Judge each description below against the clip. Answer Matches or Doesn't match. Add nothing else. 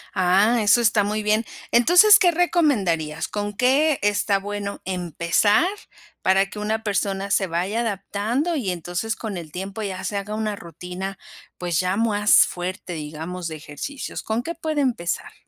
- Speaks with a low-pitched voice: Doesn't match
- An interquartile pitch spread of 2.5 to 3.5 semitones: Doesn't match